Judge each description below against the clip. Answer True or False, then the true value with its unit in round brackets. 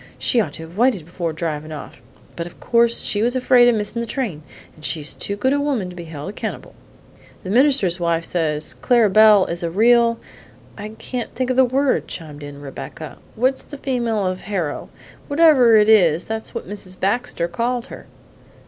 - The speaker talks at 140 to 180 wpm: False (195 wpm)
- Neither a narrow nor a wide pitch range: False (6.3 semitones)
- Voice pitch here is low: False (210 Hz)